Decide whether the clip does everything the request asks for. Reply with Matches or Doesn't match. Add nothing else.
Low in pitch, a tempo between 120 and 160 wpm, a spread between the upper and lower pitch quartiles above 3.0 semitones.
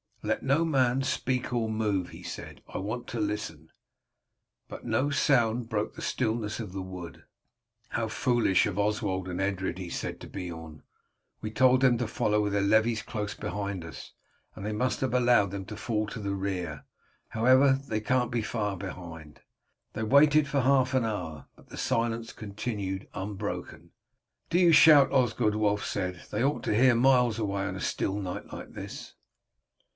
Doesn't match